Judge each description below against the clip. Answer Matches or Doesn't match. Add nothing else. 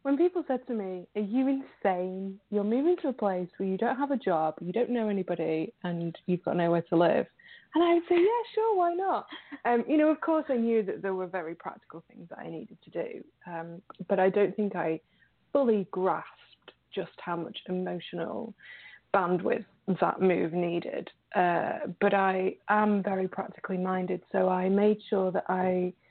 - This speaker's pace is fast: Doesn't match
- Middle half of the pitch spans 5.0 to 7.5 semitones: Matches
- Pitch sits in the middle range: Doesn't match